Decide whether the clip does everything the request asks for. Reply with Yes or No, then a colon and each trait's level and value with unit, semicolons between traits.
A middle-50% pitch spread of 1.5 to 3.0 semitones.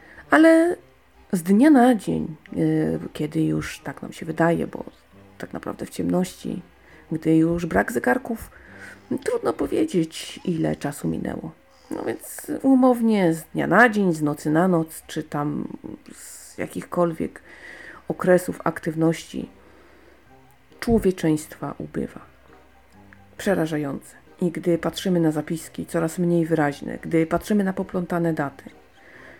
No: average, 4.2 semitones